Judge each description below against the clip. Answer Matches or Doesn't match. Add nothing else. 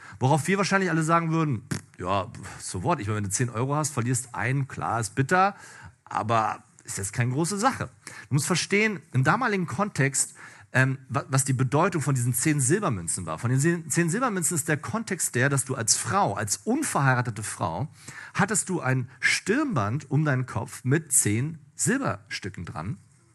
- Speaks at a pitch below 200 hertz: Matches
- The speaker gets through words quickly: Doesn't match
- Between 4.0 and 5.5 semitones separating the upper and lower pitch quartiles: Matches